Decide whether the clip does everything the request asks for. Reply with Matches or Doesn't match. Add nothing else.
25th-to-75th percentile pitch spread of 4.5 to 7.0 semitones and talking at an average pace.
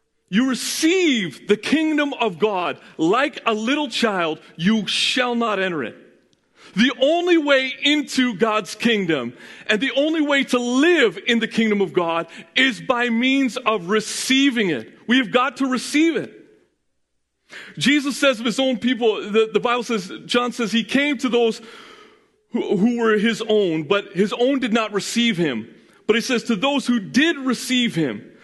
Doesn't match